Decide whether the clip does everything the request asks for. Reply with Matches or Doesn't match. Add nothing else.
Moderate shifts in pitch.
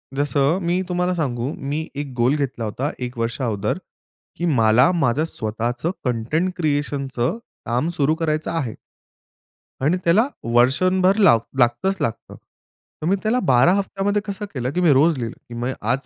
Doesn't match